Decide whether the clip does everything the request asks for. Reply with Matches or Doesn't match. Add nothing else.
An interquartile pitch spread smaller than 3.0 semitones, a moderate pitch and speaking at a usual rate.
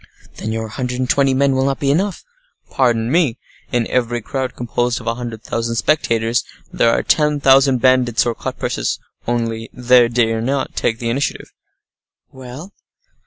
Doesn't match